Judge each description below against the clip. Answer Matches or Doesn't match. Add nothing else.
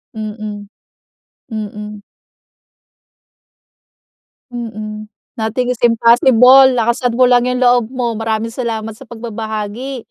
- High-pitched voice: Matches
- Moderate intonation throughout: Doesn't match